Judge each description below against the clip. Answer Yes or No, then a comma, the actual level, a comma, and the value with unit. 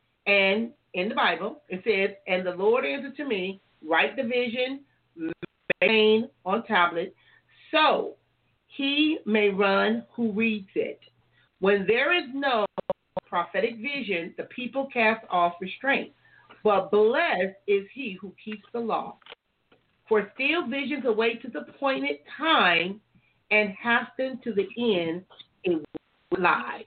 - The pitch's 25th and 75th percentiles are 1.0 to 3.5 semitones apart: No, average, 5.1 semitones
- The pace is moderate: No, slow, 130 wpm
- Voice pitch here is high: Yes, high, 215 Hz